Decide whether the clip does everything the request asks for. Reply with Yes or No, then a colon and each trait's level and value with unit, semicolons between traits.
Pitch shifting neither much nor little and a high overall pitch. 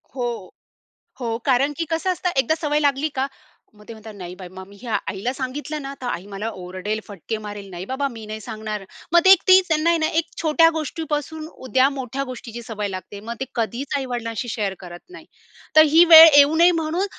No: wide, 6.5 semitones; very high, 255 Hz